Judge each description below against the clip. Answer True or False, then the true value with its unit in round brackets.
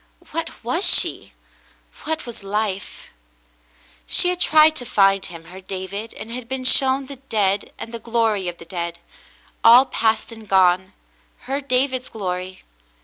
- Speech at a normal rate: True (160 wpm)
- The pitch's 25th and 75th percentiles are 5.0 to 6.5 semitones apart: True (5.5 semitones)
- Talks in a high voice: True (220 Hz)